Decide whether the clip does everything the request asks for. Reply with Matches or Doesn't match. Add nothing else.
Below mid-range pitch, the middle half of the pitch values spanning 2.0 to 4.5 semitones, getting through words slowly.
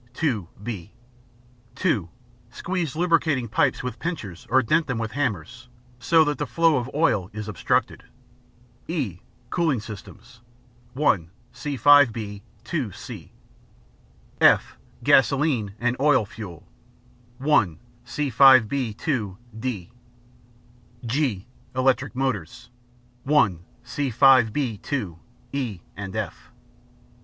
Doesn't match